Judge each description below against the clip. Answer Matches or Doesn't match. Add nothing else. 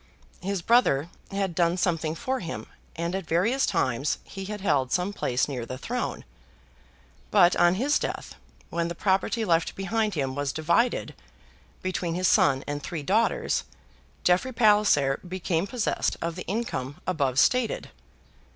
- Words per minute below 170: Matches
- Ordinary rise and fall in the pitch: Matches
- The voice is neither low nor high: Matches